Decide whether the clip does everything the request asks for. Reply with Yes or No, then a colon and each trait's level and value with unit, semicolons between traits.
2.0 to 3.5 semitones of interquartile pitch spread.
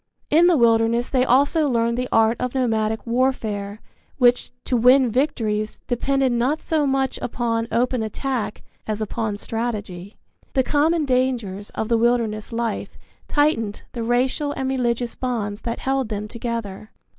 Yes: average, 3.0 semitones